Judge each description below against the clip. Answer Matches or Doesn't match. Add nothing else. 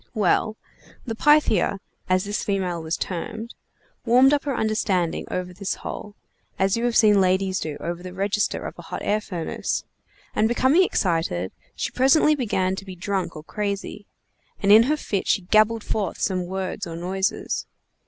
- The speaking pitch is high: Matches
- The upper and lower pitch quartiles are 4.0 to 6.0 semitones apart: Doesn't match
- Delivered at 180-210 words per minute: Doesn't match